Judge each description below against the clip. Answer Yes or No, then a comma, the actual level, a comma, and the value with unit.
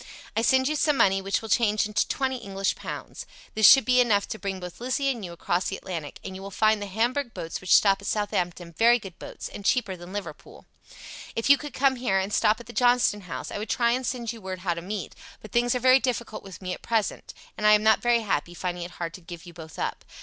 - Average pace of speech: No, fast, 260 wpm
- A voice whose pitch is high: Yes, high, 210 Hz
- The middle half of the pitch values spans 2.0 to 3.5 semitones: No, average, 4.4 semitones